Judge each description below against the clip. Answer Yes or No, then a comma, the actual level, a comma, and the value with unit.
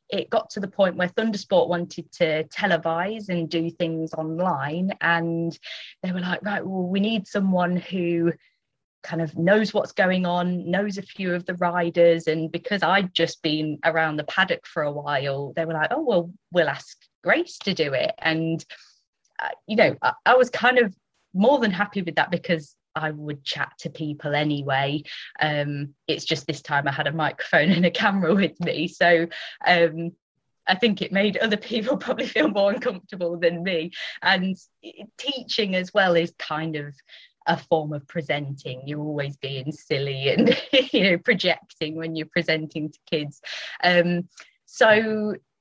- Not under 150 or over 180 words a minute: Yes, average, 175 wpm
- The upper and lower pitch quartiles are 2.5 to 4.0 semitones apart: Yes, average, 3.7 semitones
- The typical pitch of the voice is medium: Yes, medium, 170 Hz